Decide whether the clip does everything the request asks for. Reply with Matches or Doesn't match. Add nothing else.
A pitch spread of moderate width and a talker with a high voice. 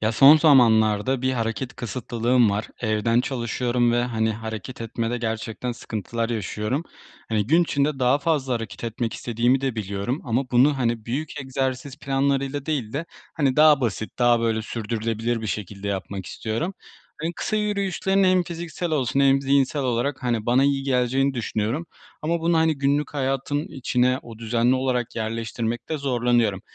Doesn't match